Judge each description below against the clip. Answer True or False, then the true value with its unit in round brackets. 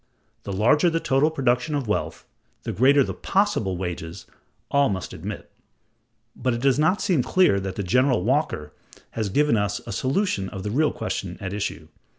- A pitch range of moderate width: False (6.9 semitones)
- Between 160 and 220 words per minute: True (170 wpm)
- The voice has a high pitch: False (120 Hz)